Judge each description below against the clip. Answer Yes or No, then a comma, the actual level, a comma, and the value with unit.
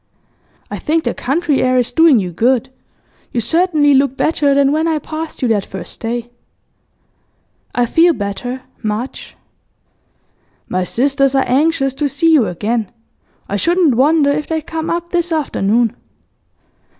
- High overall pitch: Yes, very high, 275 Hz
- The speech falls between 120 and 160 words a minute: Yes, average, 150 wpm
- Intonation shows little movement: No, average, 5.1 semitones